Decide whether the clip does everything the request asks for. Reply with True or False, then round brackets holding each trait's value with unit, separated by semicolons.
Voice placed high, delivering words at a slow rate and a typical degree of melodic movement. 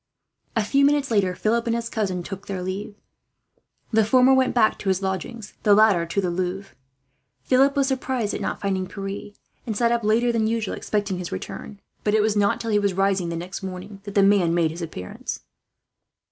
False (205 Hz; 200 wpm; 3.4 semitones)